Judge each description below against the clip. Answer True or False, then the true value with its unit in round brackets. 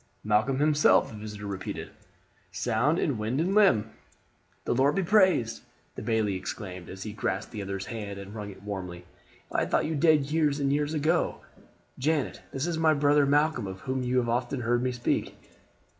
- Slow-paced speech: False (190 wpm)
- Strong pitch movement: True (6.1 semitones)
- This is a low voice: True (125 Hz)